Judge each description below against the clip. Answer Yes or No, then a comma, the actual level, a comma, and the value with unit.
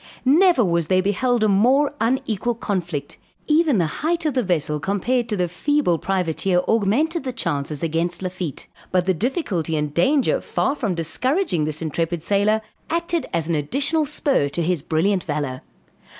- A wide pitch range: Yes, wide, 7.9 semitones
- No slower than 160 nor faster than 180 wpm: Yes, average, 165 wpm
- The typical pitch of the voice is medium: No, high, 195 Hz